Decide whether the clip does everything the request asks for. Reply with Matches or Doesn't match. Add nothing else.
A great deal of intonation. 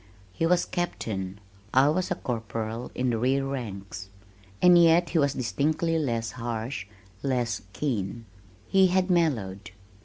Matches